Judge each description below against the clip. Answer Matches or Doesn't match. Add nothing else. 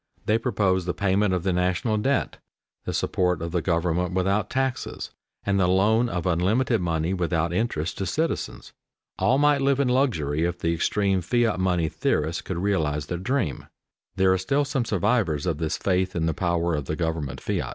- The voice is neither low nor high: Doesn't match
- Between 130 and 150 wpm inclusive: Doesn't match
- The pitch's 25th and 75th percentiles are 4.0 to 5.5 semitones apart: Matches